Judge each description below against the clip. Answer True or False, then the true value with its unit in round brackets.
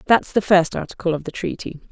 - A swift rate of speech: True (220 wpm)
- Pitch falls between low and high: True (180 Hz)